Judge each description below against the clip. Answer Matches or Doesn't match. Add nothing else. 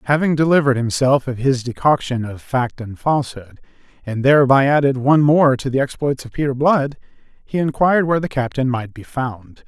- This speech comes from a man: Matches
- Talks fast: Doesn't match